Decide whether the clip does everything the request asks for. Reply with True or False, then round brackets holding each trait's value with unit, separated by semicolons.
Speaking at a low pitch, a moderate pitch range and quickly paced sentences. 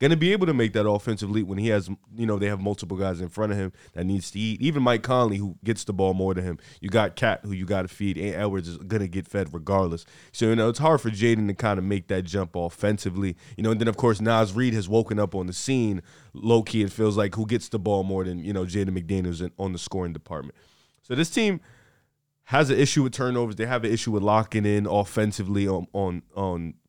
True (105 Hz; 3.1 semitones; 265 wpm)